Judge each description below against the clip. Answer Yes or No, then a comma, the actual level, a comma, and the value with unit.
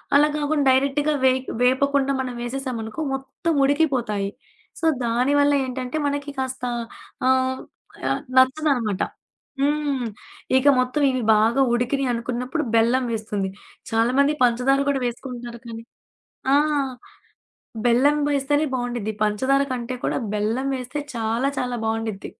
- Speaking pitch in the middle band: No, very high, 260 Hz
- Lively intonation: No, average, 3.0 semitones